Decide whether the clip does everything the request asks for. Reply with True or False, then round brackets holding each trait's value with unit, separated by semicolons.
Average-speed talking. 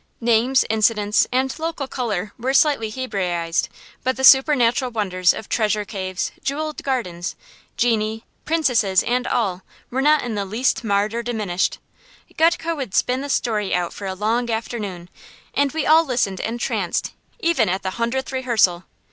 True (155 wpm)